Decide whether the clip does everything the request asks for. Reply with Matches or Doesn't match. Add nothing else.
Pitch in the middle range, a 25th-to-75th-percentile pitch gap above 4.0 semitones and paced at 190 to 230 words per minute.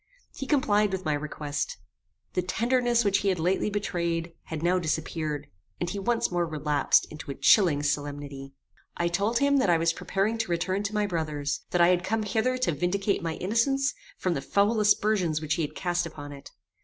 Matches